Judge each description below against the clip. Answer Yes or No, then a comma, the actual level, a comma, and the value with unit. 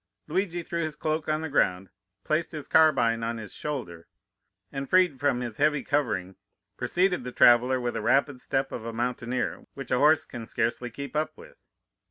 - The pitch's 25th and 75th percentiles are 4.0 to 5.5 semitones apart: Yes, average, 4.5 semitones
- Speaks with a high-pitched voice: No, low, 135 Hz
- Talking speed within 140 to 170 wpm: No, average, 185 wpm